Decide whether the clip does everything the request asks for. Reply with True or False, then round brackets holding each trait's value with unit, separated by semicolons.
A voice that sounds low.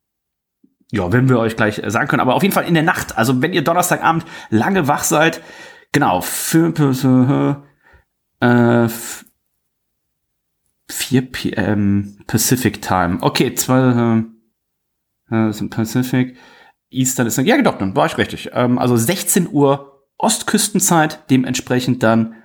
True (125 Hz)